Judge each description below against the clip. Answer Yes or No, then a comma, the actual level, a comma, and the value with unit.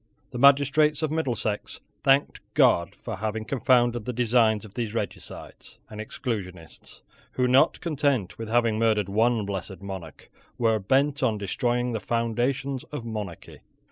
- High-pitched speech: No, low, 115 Hz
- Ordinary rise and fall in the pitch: Yes, average, 3.6 semitones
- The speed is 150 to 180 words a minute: No, average, 140 wpm